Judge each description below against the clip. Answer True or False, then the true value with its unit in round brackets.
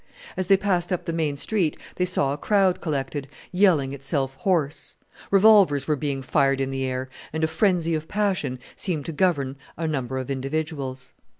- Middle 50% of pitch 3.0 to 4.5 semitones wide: False (4.9 semitones)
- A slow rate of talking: False (180 wpm)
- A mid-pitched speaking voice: True (155 Hz)